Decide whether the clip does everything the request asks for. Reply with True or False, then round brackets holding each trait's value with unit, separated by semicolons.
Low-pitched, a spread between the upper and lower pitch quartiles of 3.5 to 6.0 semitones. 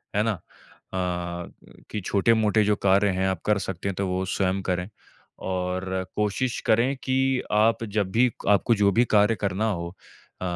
False (100 Hz; 3.0 semitones)